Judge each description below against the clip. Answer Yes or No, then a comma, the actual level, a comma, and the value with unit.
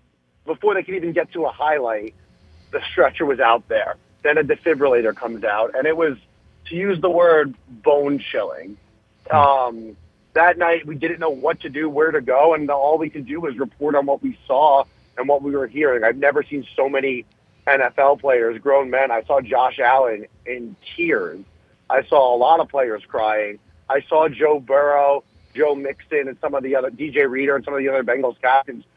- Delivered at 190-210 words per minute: Yes, average, 200 wpm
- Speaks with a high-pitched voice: No, medium, 140 Hz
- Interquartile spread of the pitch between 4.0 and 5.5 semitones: Yes, average, 4.6 semitones